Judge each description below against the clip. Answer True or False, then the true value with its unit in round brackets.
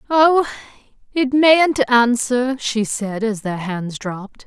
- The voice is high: True (245 Hz)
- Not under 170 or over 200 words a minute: False (135 wpm)